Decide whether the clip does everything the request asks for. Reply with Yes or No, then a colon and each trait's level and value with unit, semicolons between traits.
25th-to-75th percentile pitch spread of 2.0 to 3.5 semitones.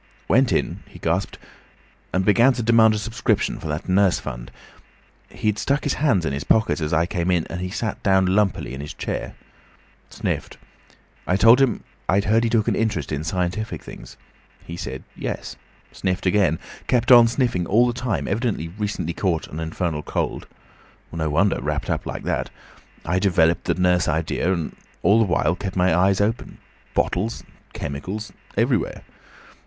No: average, 4.9 semitones